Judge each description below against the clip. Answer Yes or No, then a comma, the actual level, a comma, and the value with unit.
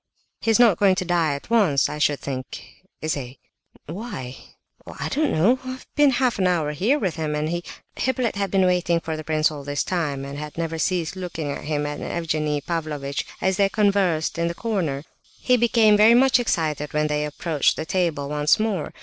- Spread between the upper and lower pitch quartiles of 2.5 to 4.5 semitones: No, average, 5.3 semitones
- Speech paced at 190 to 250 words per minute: Yes, average, 200 wpm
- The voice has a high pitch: No, medium, 165 Hz